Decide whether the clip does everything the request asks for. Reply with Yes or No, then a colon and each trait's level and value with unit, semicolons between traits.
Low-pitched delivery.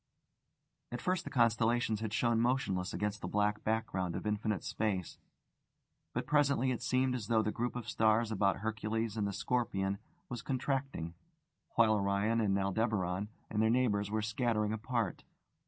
Yes: low, 110 Hz